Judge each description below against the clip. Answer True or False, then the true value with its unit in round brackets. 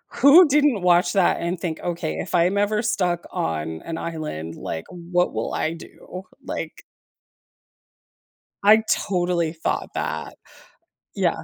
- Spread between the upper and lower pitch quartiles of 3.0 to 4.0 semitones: True (3.7 semitones)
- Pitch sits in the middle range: True (175 Hz)